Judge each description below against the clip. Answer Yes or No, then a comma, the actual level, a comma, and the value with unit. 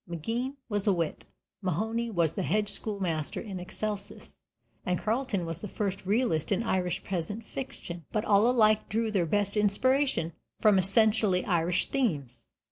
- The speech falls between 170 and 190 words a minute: No, average, 150 wpm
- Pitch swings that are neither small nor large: Yes, average, 3.9 semitones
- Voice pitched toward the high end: Yes, high, 200 Hz